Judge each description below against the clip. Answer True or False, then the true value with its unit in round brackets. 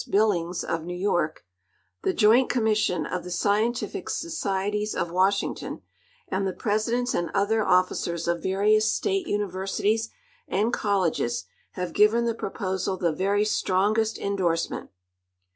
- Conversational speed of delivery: False (130 wpm)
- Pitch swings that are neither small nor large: True (3.1 semitones)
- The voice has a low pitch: False (200 Hz)